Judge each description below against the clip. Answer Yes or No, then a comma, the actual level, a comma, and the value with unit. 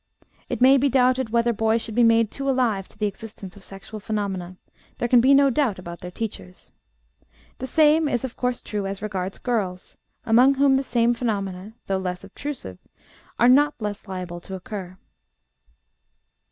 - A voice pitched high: Yes, high, 225 Hz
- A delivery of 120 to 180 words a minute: Yes, average, 175 wpm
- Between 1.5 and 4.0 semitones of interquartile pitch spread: No, average, 4.7 semitones